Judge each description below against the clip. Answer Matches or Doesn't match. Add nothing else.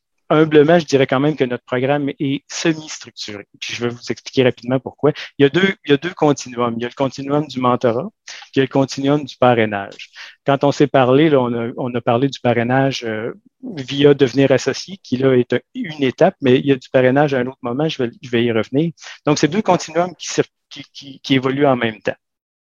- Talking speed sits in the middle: Doesn't match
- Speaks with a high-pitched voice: Doesn't match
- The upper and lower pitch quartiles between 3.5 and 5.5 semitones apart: Doesn't match